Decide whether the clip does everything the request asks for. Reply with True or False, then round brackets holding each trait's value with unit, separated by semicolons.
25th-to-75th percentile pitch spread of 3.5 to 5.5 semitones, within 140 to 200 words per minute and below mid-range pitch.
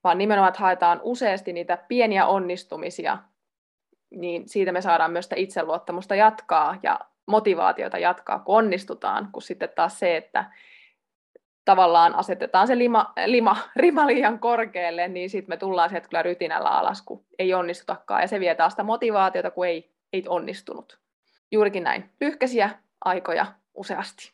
False (3.8 semitones; 150 wpm; 190 Hz)